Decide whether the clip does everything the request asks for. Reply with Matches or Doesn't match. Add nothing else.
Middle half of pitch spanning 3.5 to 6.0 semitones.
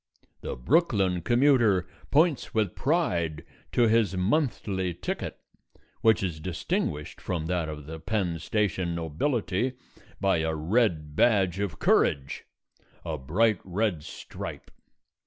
Matches